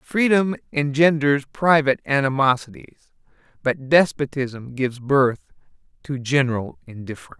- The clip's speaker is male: Yes, male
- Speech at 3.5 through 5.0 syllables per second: Yes, 4.7 syllables/s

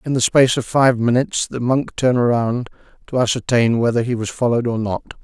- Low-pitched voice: Yes, low, 120 Hz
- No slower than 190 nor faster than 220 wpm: Yes, fast, 205 wpm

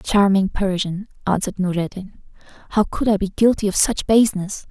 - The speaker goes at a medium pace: Yes, average, 155 wpm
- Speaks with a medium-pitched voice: No, high, 195 Hz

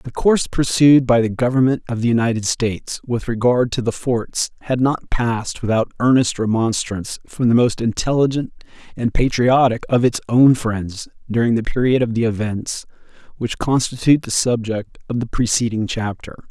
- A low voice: Yes, low, 120 Hz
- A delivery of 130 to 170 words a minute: Yes, average, 165 wpm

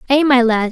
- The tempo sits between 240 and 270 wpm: Yes, fast, 250 wpm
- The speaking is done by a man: No, female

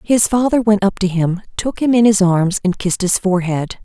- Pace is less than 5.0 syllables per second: No, 5.4 syllables/s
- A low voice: No, high, 200 Hz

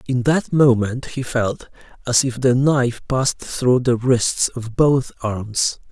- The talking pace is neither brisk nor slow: Yes, average, 160 wpm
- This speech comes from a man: Yes, male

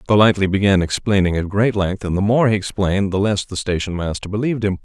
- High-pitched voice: No, low, 100 Hz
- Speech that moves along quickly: Yes, fast, 225 wpm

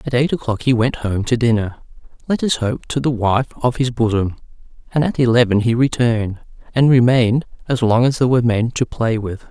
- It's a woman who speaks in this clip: No, male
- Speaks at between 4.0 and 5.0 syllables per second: No, 5.6 syllables/s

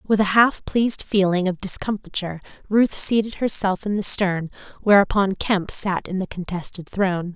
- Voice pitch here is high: Yes, high, 195 Hz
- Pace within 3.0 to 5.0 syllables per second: Yes, 4.9 syllables/s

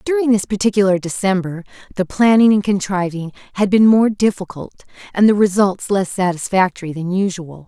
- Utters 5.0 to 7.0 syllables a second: Yes, 5.5 syllables/s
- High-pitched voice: Yes, high, 195 Hz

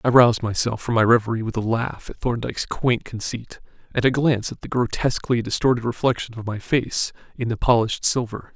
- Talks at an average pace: Yes, average, 195 wpm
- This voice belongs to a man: Yes, male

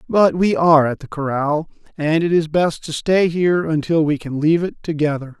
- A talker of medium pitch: Yes, medium, 160 Hz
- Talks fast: Yes, fast, 210 wpm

